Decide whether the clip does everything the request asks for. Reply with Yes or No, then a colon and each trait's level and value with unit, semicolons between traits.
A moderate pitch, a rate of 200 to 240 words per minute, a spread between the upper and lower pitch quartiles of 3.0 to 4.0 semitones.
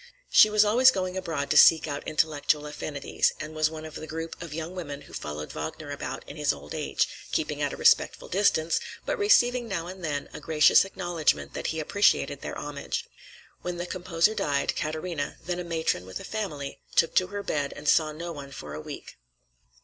Yes: medium, 160 Hz; fast, 205 wpm; average, 3.7 semitones